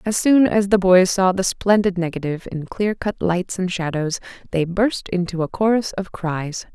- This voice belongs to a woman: Yes, female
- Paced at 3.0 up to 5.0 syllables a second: Yes, 4.7 syllables/s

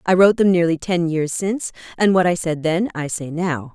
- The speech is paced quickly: Yes, fast, 240 wpm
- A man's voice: No, female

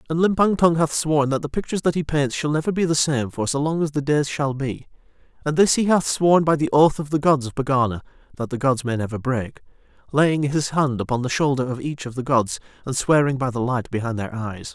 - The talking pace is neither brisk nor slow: No, fast, 250 wpm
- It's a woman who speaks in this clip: No, male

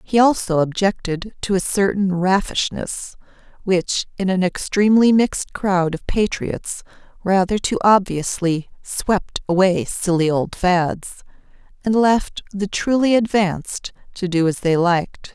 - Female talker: Yes, female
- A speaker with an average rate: No, slow, 130 wpm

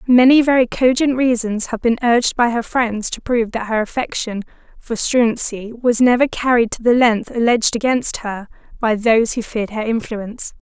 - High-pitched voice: Yes, high, 235 Hz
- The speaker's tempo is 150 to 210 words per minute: Yes, average, 180 wpm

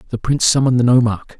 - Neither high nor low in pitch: No, low, 120 Hz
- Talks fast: Yes, fast, 215 wpm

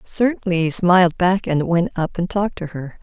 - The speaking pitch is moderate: Yes, medium, 175 Hz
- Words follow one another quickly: Yes, fast, 220 wpm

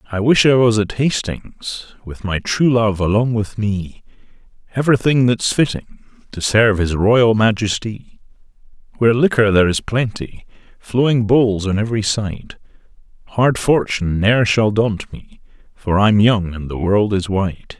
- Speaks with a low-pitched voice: Yes, low, 110 Hz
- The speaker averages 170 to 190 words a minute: No, average, 150 wpm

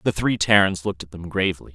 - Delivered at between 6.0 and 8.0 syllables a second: Yes, 6.8 syllables/s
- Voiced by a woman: No, male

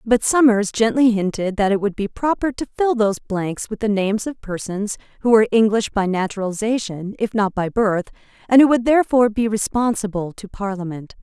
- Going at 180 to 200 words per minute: Yes, average, 185 wpm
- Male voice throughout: No, female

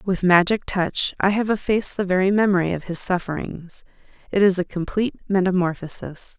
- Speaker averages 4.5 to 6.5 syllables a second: Yes, 5.5 syllables/s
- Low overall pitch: No, medium, 185 Hz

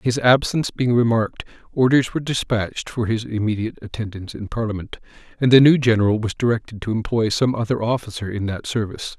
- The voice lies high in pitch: No, low, 115 Hz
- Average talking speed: Yes, average, 175 wpm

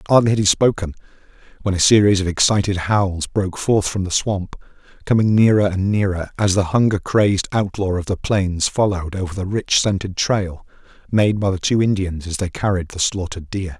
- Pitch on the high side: No, very low, 95 Hz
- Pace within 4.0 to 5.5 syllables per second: Yes, 5.4 syllables/s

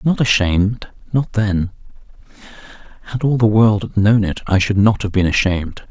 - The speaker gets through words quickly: No, average, 175 wpm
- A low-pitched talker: Yes, low, 105 Hz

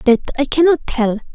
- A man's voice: No, female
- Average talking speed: Yes, average, 180 wpm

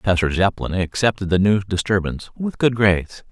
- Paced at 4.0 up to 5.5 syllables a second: No, 5.7 syllables/s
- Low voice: Yes, low, 100 Hz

